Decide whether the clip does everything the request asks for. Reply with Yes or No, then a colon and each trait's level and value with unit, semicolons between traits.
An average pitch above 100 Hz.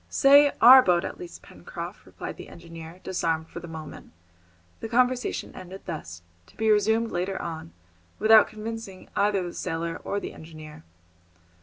Yes: medium, 185 Hz